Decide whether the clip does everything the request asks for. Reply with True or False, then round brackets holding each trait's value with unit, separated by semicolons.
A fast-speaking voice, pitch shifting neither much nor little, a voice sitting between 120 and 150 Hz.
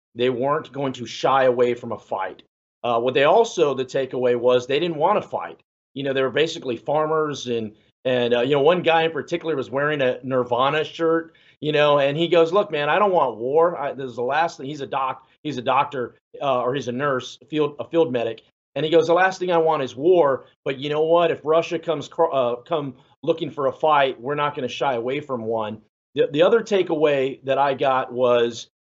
True (235 wpm; 4.4 semitones; 140 Hz)